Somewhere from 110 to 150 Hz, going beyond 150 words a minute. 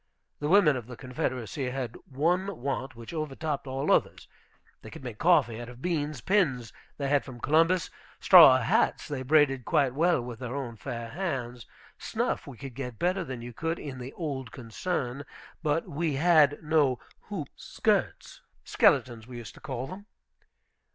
Yes: low, 135 Hz; average, 170 wpm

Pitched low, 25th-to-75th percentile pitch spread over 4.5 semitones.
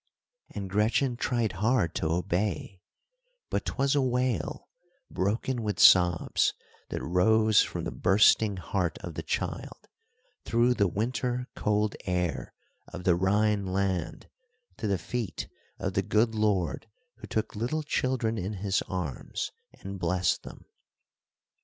No: low, 105 Hz; average, 3.9 semitones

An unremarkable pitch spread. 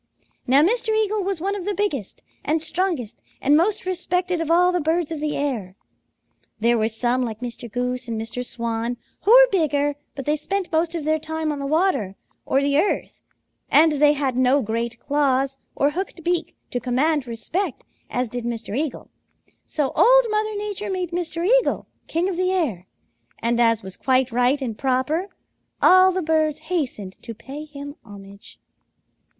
No: wide, 6.4 semitones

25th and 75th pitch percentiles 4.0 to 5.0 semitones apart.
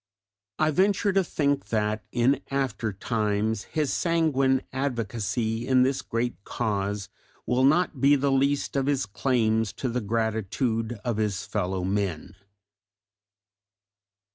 Yes: average, 4.4 semitones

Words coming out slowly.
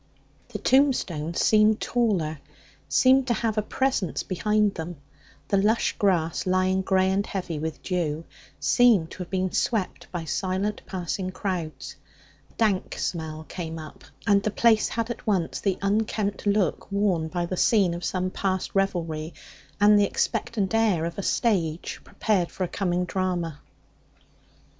No: average, 150 wpm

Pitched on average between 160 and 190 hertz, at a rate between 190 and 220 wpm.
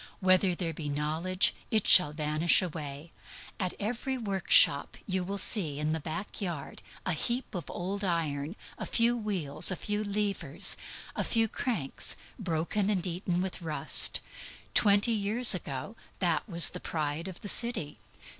No: medium, 185 Hz; average, 155 wpm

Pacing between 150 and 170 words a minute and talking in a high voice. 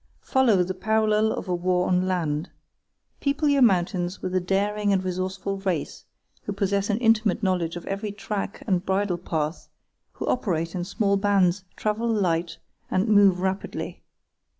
Yes: average, 155 wpm; high, 195 Hz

